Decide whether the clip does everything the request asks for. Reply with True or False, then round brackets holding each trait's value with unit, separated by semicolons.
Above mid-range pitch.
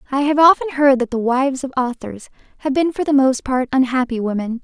True (265 Hz)